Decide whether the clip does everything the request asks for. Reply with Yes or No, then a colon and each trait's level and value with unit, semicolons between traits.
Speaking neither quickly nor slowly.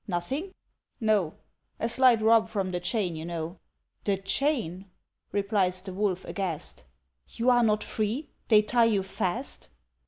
Yes: average, 145 wpm